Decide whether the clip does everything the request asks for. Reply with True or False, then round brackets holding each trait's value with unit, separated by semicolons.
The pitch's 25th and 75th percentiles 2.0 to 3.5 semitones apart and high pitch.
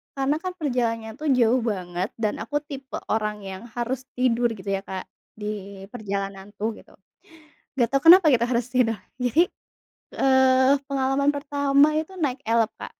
False (4.0 semitones; 250 Hz)